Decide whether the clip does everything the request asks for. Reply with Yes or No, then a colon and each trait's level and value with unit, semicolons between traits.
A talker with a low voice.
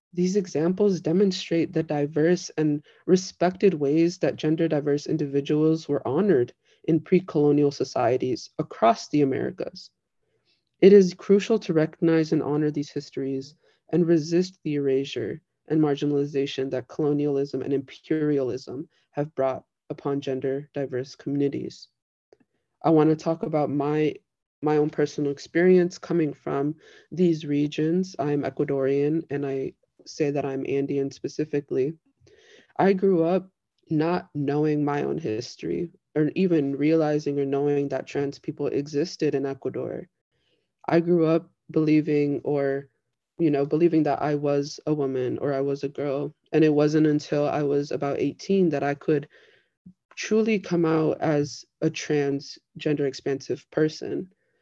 No: medium, 150 Hz